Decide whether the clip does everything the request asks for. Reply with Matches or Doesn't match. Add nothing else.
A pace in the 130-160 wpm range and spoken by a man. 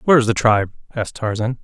Doesn't match